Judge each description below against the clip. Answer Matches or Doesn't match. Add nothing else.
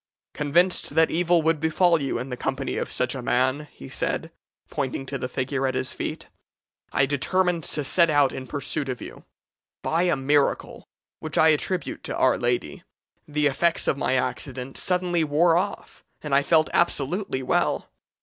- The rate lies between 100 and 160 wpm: Doesn't match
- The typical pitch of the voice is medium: Matches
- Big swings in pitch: Doesn't match